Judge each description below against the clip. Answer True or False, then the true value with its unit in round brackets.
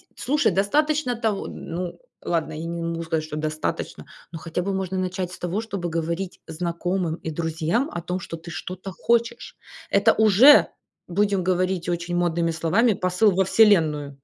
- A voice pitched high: False (180 Hz)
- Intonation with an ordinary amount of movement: True (3.1 semitones)